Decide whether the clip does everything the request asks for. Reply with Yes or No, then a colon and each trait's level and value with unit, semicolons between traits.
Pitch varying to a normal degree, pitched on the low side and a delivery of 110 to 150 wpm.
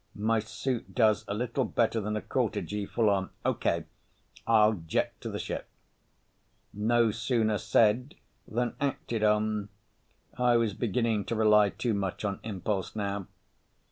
No: narrow, 2.1 semitones; low, 110 Hz; average, 140 wpm